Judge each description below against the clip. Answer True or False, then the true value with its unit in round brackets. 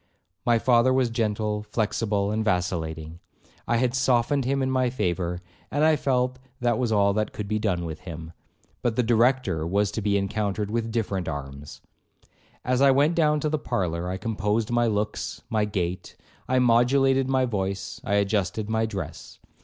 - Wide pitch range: False (4.2 semitones)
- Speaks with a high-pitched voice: False (110 Hz)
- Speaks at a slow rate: False (175 wpm)